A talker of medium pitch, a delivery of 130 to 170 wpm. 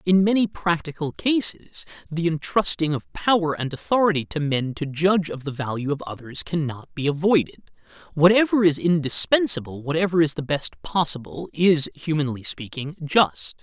Yes: medium, 160 Hz; average, 150 wpm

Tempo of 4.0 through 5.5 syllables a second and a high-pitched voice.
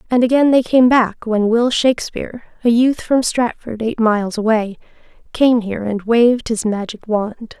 Yes: 4.9 syllables/s; high, 230 Hz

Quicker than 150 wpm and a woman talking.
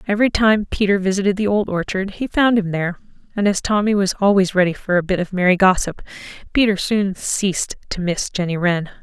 Yes: average, 200 wpm; female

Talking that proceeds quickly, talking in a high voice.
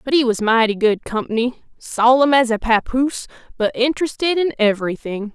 No: average, 155 wpm; high, 240 Hz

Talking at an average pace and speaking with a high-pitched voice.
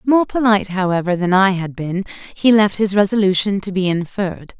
Yes: average, 185 wpm; high, 195 Hz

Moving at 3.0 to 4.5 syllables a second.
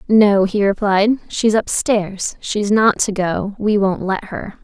Yes: 3.6 syllables/s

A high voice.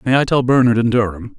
No: low, 120 Hz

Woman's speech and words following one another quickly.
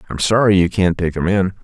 No: male; fast, 255 wpm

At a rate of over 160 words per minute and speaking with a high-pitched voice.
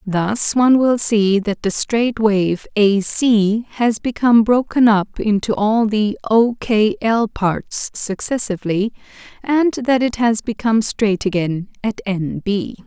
No: average, 150 wpm; high, 220 Hz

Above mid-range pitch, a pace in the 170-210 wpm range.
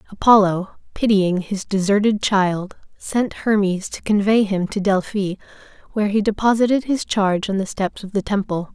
No: high, 200 Hz; average, 160 wpm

